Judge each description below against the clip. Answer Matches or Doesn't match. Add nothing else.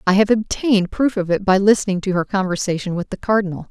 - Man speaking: Doesn't match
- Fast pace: Matches